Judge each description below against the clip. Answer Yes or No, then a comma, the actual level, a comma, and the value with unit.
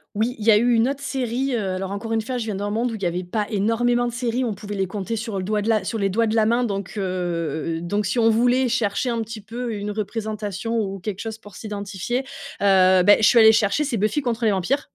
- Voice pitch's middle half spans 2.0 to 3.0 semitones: Yes, average, 2.7 semitones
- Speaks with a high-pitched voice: Yes, high, 215 Hz